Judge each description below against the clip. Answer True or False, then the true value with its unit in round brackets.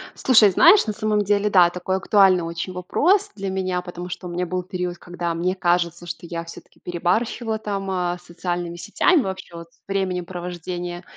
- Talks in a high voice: False (180 Hz)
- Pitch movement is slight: True (2.1 semitones)